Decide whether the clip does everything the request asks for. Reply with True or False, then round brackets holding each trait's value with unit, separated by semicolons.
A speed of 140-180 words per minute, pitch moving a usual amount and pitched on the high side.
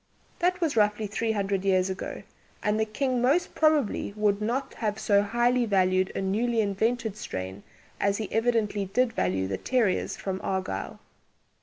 True (160 wpm; 3.6 semitones; 210 Hz)